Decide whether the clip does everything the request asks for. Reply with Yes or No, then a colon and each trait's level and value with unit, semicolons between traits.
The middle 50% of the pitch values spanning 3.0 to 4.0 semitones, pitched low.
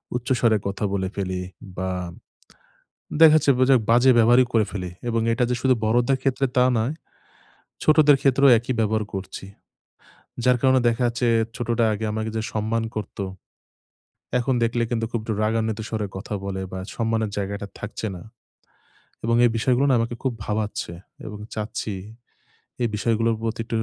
No: narrow, 2.6 semitones; low, 115 Hz